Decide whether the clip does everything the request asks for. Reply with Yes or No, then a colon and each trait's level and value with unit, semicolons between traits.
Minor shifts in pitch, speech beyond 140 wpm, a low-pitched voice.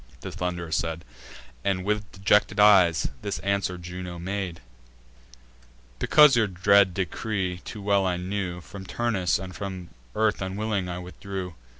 No: narrow, 2.2 semitones; slow, 135 wpm; very low, 95 Hz